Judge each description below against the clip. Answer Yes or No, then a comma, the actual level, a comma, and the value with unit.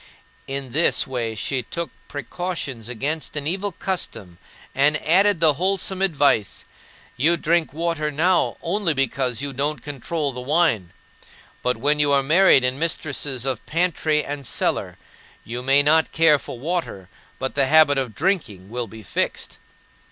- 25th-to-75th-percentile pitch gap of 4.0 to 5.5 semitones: Yes, average, 4.3 semitones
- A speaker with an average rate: Yes, average, 150 wpm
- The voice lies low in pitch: No, medium, 145 Hz